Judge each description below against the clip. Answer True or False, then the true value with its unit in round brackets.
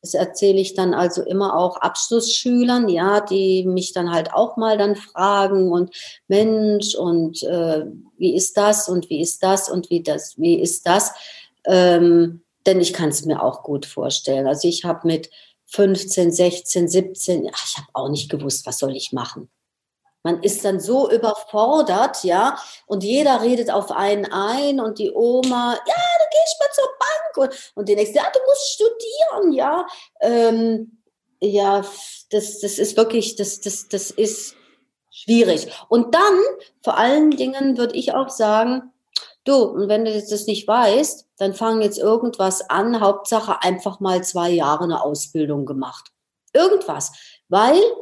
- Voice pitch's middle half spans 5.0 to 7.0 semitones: True (5.4 semitones)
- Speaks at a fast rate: False (165 wpm)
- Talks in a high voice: True (205 Hz)